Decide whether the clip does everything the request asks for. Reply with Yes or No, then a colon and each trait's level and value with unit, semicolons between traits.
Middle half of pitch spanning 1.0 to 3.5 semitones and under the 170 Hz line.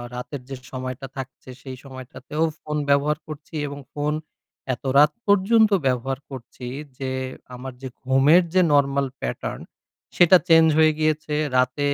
Yes: average, 2.8 semitones; medium, 140 Hz